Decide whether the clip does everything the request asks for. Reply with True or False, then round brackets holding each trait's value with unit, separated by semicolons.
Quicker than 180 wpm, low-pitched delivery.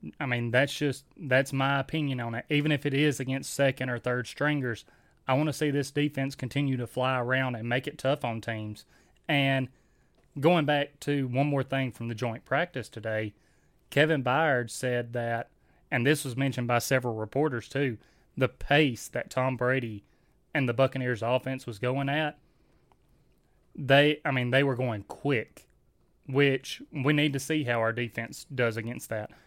False (175 wpm; 130 Hz)